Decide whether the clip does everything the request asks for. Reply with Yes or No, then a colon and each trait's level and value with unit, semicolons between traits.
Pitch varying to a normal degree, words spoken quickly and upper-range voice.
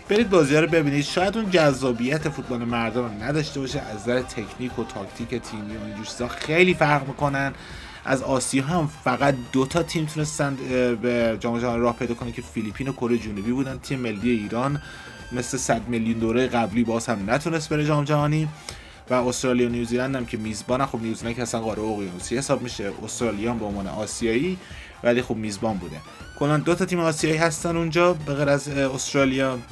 No: average, 3.9 semitones; fast, 185 wpm; low, 125 Hz